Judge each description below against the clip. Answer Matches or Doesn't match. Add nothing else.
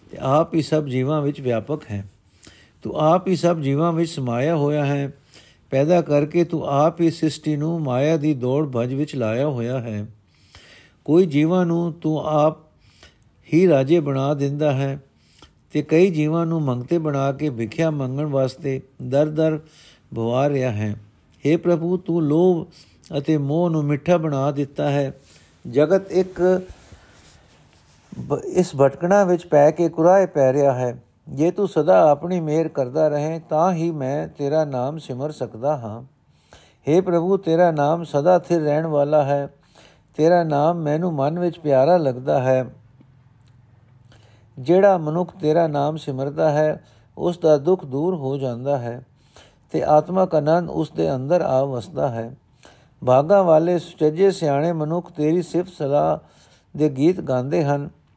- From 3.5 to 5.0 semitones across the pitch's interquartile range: Matches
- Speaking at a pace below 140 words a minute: Doesn't match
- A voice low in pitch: Doesn't match